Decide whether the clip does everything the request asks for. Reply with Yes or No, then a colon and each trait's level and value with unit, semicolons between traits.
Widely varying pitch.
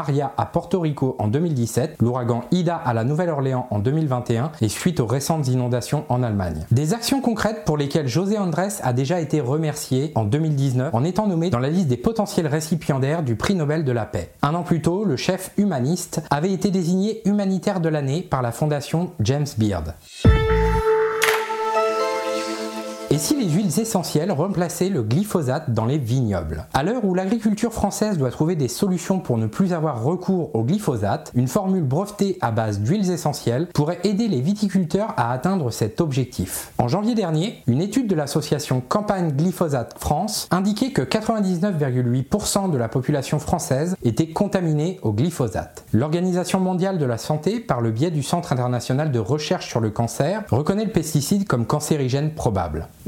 Yes: wide, 7.1 semitones